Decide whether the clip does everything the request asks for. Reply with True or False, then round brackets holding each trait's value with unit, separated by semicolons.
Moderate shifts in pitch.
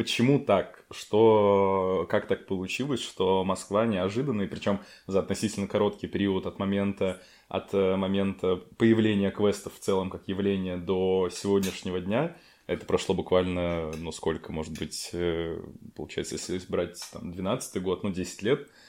False (1.9 semitones)